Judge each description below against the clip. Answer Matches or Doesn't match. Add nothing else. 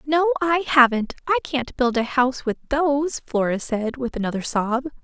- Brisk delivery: Doesn't match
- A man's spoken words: Doesn't match